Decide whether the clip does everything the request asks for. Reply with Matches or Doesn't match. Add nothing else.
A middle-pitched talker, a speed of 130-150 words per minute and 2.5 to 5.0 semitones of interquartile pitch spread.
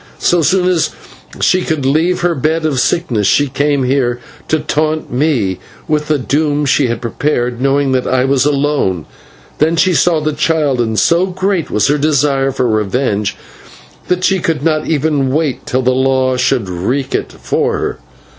Doesn't match